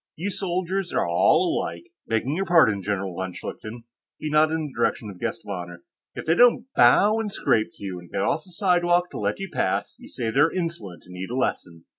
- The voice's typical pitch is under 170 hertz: Yes, medium, 140 Hz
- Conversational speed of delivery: No, fast, 230 wpm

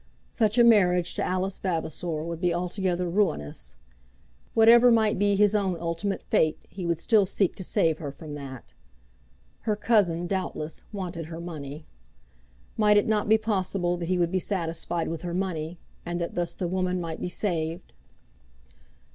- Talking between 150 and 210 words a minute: Yes, average, 165 wpm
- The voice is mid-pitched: Yes, medium, 180 Hz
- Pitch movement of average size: Yes, average, 3.2 semitones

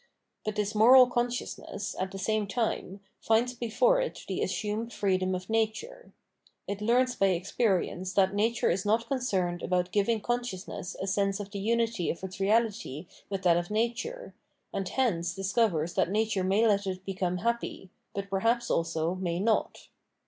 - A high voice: Yes, high, 205 Hz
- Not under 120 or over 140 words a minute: No, average, 165 wpm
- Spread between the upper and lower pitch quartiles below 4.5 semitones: Yes, average, 3.6 semitones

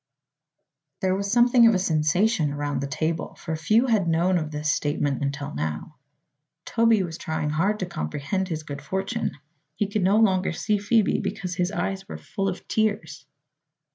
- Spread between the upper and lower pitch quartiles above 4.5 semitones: Yes, average, 5.1 semitones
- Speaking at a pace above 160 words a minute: Yes, average, 170 wpm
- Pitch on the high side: No, medium, 180 Hz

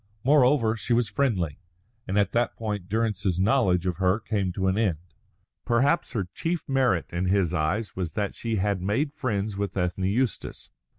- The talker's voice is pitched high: No, low, 105 Hz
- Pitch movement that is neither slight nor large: Yes, average, 4.0 semitones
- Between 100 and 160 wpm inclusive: No, average, 175 wpm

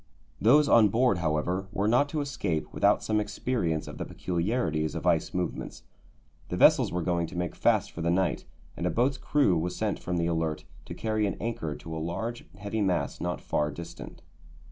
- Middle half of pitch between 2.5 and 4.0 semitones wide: No, average, 5.1 semitones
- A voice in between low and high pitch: No, very low, 90 Hz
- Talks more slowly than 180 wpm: No, average, 195 wpm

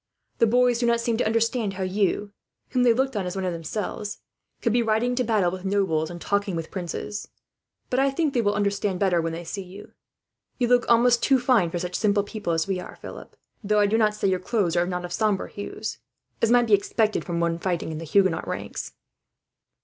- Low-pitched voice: No, high, 205 Hz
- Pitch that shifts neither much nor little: Yes, average, 4.3 semitones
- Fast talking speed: Yes, fast, 225 wpm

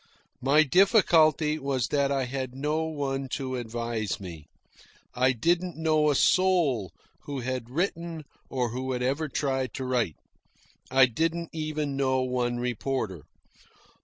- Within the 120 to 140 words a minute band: Yes, slow, 135 wpm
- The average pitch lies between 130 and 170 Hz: Yes, low, 135 Hz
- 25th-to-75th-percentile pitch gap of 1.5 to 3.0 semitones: No, average, 3.8 semitones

